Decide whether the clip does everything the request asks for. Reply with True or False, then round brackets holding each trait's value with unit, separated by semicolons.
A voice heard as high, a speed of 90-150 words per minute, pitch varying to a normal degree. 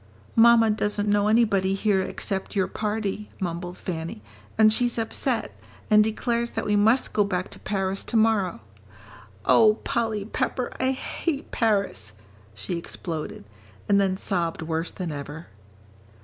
True (205 Hz; 140 wpm; 3.5 semitones)